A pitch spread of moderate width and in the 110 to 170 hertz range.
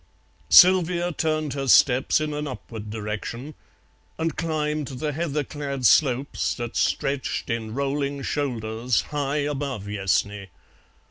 Yes: average, 4.1 semitones; medium, 140 Hz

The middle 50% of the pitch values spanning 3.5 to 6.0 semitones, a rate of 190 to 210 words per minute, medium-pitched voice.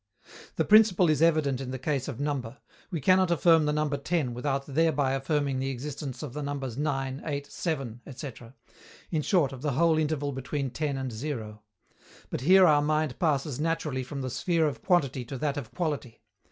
No: average, 2.8 semitones; average, 195 wpm; medium, 145 Hz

